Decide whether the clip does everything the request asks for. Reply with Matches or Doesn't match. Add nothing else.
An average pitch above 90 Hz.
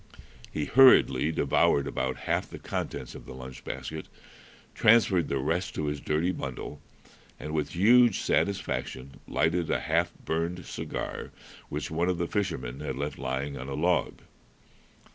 Doesn't match